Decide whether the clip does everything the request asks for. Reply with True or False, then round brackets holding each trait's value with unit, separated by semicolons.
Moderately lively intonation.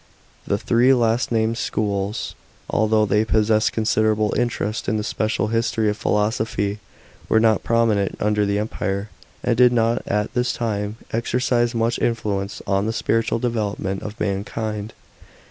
False (1.7 semitones)